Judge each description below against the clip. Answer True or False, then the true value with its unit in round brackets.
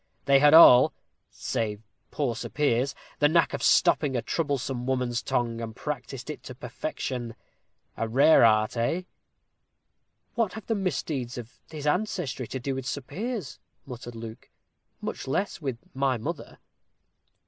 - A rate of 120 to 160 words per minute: True (150 wpm)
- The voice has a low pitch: True (130 Hz)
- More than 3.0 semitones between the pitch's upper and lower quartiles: True (4.1 semitones)